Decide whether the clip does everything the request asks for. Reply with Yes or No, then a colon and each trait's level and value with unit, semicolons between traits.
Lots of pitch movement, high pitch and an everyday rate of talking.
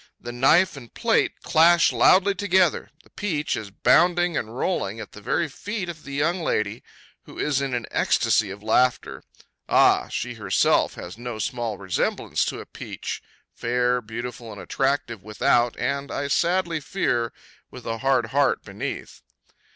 No: wide, 6.3 semitones; low, 130 Hz; average, 160 wpm